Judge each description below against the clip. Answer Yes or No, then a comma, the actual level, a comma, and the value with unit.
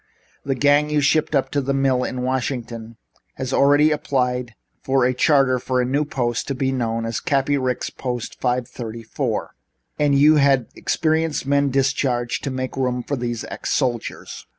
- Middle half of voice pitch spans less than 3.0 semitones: Yes, narrow, 2.4 semitones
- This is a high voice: No, low, 130 Hz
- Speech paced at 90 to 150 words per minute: No, average, 175 wpm